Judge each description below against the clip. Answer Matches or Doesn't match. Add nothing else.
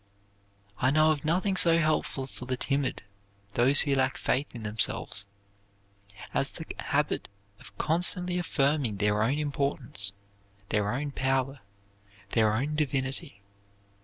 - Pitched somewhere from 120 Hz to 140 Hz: Matches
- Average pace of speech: Doesn't match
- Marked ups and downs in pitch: Doesn't match